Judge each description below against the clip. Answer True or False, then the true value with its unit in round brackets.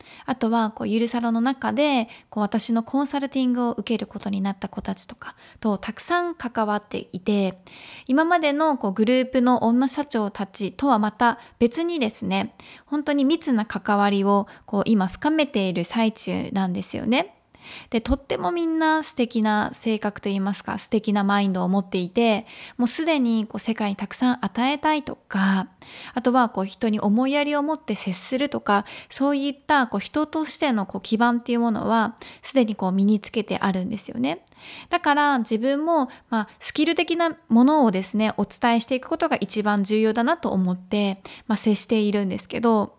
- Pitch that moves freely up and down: False (4.8 semitones)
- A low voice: False (230 Hz)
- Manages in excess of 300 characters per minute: True (365 characters per minute)